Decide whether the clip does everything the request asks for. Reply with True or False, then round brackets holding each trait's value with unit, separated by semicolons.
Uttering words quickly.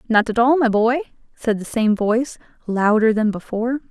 False (185 wpm)